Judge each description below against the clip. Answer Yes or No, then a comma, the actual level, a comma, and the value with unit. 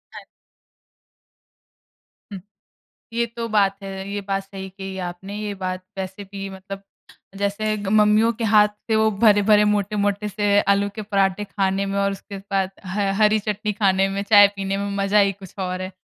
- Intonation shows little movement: Yes, narrow, 1.3 semitones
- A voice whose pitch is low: No, high, 200 Hz